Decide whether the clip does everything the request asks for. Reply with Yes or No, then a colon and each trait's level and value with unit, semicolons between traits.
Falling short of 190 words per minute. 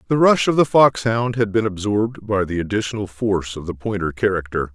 No: average, 200 wpm